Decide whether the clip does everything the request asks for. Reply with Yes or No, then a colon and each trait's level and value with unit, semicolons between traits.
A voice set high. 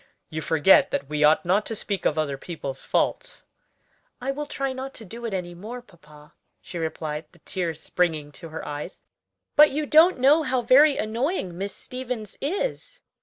Yes: high, 200 Hz